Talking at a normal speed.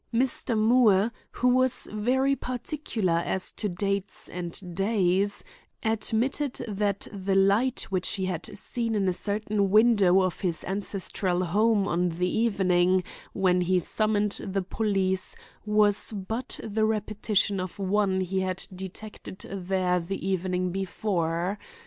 No: slow, 130 wpm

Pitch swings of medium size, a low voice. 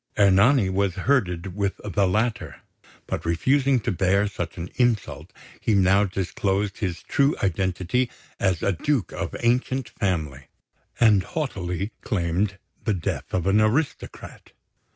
Yes: average, 4.0 semitones; low, 100 Hz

